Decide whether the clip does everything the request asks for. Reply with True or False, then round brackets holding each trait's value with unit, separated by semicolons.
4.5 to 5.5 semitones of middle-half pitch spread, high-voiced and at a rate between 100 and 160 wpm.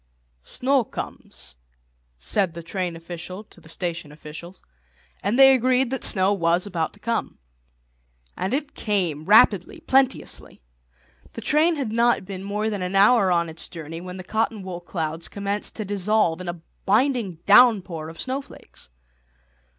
True (4.8 semitones; 195 Hz; 150 wpm)